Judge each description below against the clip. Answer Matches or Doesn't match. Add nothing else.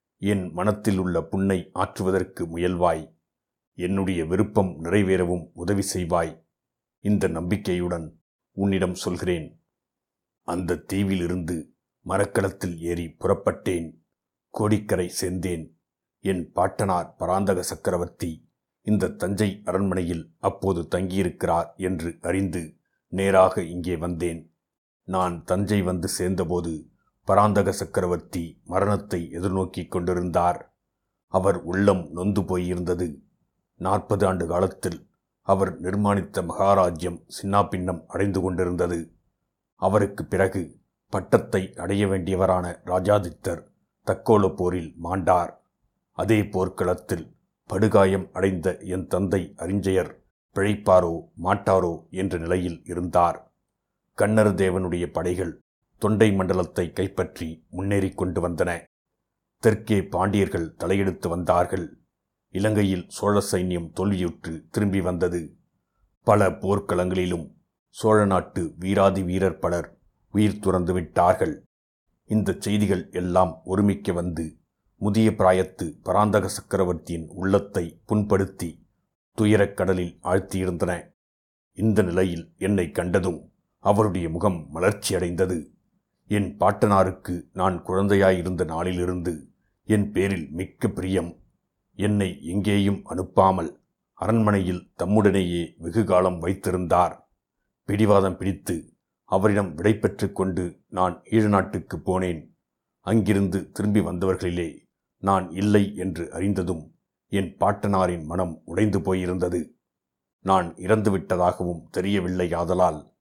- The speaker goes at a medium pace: Matches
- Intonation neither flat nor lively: Doesn't match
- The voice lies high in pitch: Doesn't match